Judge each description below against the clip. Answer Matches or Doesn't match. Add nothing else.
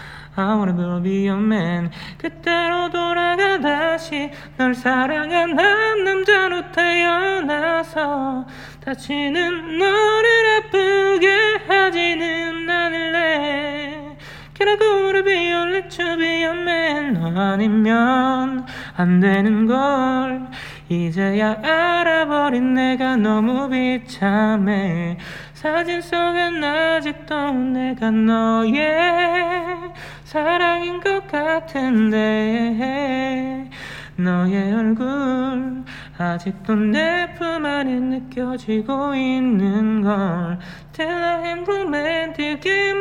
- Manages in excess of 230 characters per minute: Doesn't match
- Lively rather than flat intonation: Matches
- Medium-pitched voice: Doesn't match